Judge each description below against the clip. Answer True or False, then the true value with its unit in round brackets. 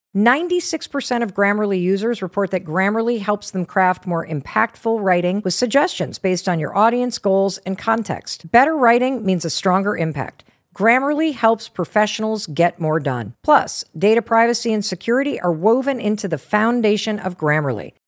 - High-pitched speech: True (205 Hz)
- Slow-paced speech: False (155 wpm)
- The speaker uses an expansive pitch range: False (4.3 semitones)